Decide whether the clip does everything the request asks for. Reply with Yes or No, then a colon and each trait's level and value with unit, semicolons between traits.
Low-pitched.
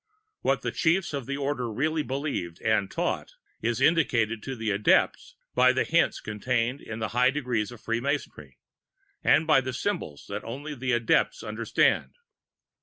Yes: low, 125 Hz